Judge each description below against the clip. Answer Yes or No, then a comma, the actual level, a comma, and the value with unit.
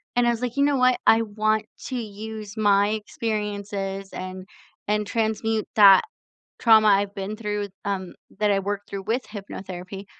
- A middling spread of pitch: No, narrow, 1.9 semitones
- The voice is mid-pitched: No, high, 210 Hz